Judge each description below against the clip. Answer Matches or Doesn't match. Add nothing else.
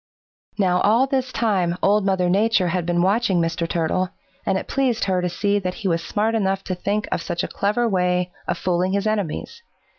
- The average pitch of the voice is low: Doesn't match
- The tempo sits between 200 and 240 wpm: Matches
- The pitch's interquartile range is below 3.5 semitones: Matches